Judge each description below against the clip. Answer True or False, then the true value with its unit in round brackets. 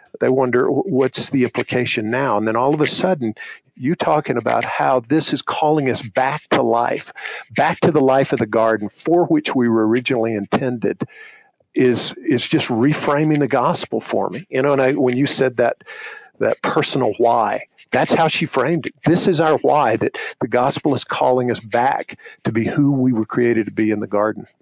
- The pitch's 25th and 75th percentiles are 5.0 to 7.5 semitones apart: False (3.7 semitones)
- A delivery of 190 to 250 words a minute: True (200 wpm)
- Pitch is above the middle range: False (125 Hz)